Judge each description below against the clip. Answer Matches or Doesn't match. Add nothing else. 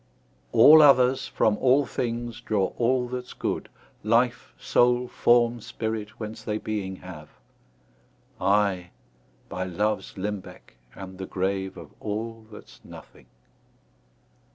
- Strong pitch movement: Doesn't match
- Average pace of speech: Doesn't match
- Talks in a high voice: Doesn't match